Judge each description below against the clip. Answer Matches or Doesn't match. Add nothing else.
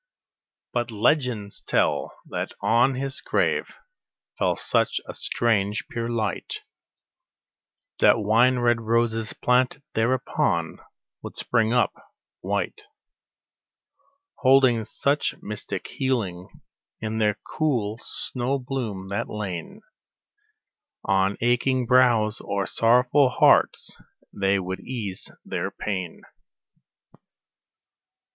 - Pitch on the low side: Matches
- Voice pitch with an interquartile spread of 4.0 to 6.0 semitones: Doesn't match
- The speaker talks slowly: Matches